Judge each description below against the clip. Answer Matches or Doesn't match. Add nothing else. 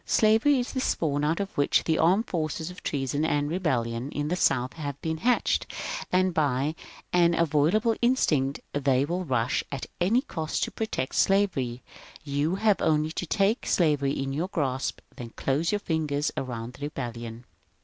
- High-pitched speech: Doesn't match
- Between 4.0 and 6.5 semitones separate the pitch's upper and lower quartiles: Matches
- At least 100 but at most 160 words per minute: Doesn't match